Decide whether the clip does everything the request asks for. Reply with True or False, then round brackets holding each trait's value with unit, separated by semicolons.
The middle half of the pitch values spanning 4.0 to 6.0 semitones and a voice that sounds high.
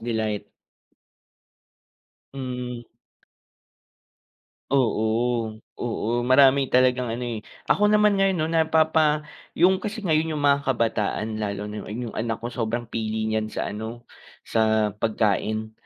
False (4.4 semitones; 120 Hz)